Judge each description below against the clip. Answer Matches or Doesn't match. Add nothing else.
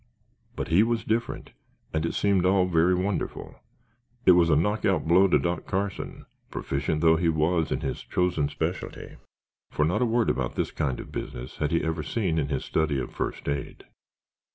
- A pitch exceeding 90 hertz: Doesn't match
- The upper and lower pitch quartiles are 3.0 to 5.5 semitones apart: Matches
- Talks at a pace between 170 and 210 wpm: Matches